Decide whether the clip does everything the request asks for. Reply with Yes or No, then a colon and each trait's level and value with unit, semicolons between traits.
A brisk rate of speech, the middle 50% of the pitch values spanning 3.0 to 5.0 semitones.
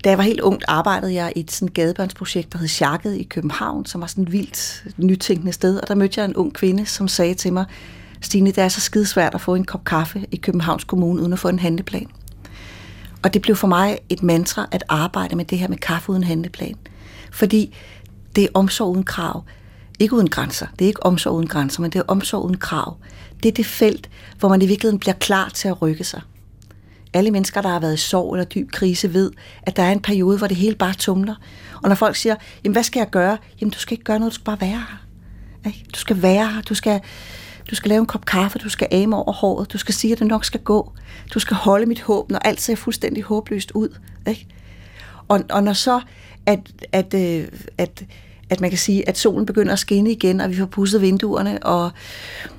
Yes: fast, 235 wpm; average, 4.0 semitones